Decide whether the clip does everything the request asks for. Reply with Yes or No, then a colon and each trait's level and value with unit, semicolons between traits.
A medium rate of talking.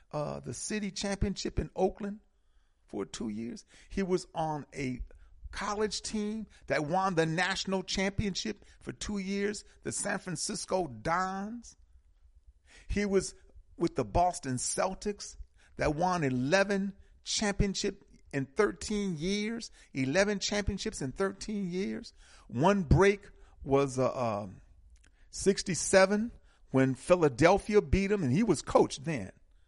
No: slow, 120 wpm